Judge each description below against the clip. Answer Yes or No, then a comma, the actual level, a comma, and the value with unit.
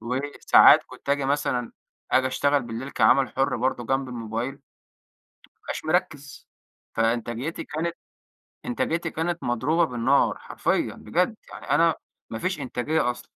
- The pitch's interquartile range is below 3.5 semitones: No, average, 4.2 semitones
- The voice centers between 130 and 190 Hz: Yes, low, 135 Hz